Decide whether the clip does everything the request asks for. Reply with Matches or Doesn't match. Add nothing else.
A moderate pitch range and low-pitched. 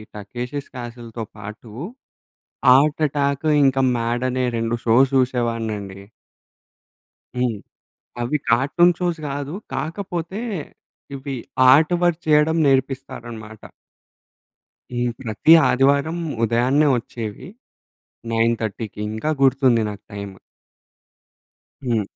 Matches